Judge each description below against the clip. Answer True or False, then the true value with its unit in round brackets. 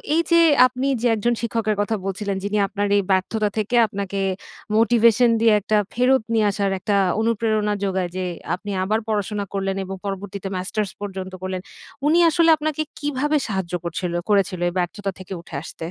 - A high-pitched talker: True (205 Hz)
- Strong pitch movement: False (3.0 semitones)